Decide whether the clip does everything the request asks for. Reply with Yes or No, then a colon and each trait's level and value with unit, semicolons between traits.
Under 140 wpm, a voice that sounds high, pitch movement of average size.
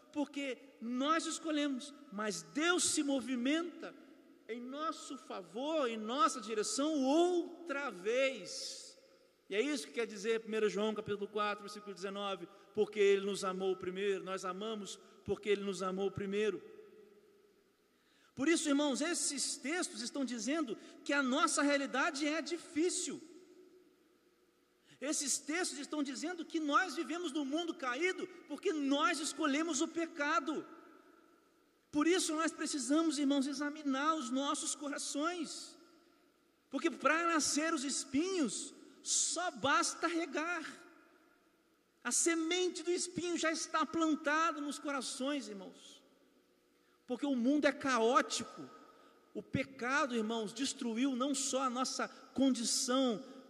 Yes: slow, 120 wpm; very high, 300 Hz; average, 4.5 semitones